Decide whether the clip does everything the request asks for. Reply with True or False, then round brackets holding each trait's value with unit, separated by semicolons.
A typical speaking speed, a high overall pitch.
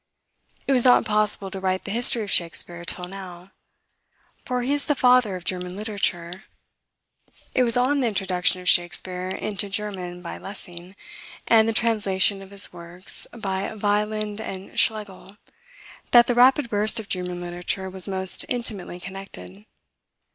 True (155 wpm; 195 Hz)